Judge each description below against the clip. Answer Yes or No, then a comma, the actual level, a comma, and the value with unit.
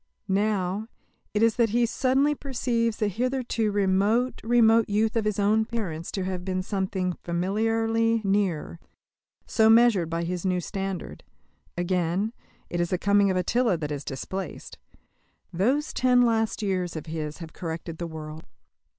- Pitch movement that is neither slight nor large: Yes, average, 4.2 semitones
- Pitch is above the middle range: Yes, high, 200 Hz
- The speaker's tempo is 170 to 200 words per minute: No, average, 150 wpm